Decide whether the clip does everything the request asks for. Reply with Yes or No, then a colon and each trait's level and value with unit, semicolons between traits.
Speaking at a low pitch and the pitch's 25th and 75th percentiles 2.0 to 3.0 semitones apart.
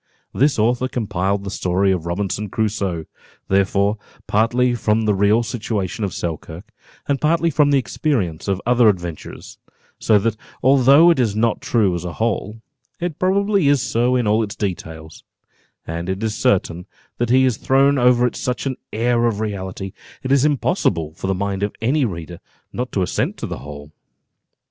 No: low, 110 Hz; average, 4.8 semitones